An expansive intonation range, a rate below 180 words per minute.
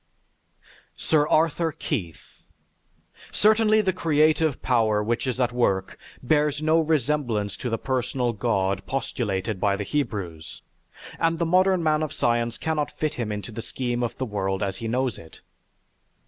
Yes: wide, 6.6 semitones; average, 150 wpm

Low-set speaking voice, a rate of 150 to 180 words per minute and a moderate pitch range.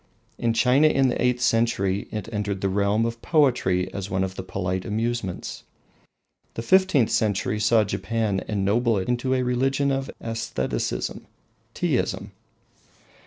No: low, 115 Hz; average, 140 wpm; average, 4.0 semitones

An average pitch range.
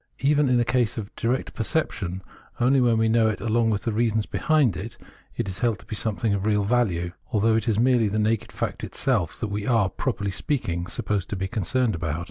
Yes: average, 3.1 semitones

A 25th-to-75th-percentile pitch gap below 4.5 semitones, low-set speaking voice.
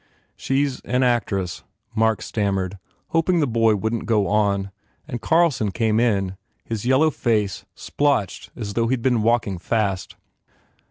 Yes: average, 3.8 semitones; low, 110 Hz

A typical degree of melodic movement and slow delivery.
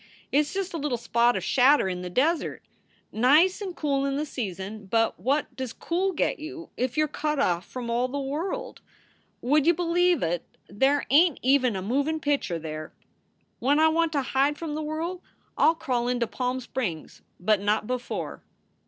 No: average, 4.9 semitones; average, 195 wpm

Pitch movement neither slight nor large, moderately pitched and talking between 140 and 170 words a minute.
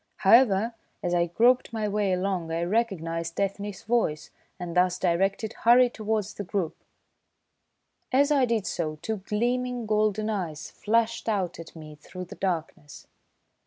No: average, 4.4 semitones; high, 200 Hz; average, 145 wpm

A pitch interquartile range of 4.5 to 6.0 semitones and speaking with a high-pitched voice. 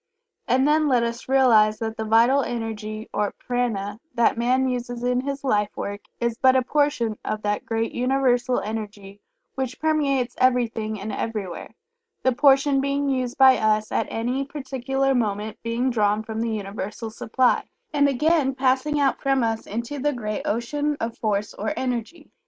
No: average, 3.5 semitones; high, 245 Hz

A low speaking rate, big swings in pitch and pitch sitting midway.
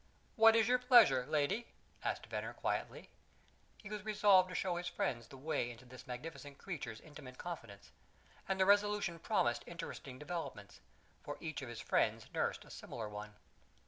No: average, 165 wpm; wide, 8.0 semitones; medium, 160 Hz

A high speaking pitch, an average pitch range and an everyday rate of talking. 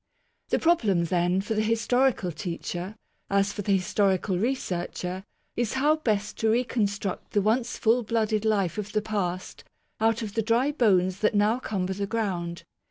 Yes: high, 210 Hz; average, 3.3 semitones; average, 165 wpm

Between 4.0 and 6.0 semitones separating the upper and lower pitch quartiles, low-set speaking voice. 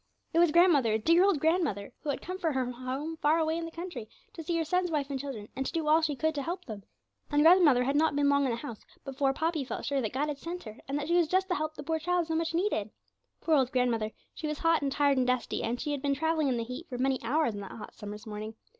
No: average, 4.4 semitones; very high, 290 Hz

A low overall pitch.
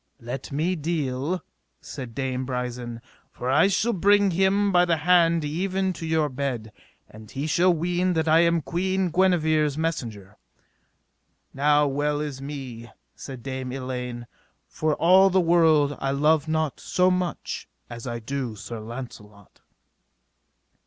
No: medium, 150 Hz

